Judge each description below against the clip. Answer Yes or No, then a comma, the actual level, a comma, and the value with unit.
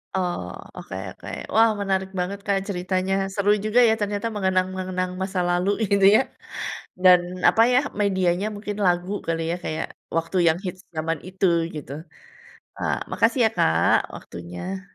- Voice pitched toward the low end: No, medium, 185 Hz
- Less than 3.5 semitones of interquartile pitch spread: Yes, narrow, 2.4 semitones